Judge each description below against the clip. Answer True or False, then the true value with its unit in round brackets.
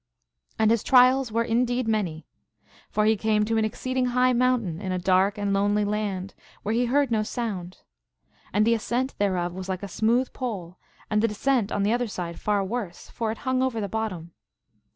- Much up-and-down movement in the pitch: False (3.5 semitones)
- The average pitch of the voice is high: True (215 Hz)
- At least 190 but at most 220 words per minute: True (205 wpm)